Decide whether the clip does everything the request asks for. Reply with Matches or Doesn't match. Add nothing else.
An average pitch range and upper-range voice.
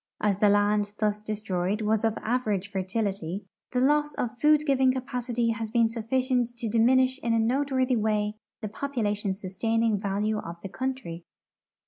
Matches